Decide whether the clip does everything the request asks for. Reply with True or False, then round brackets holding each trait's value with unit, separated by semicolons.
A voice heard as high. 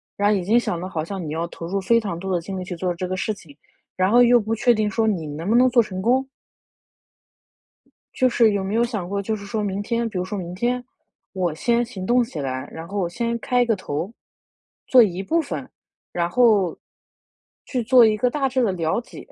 True (205 Hz)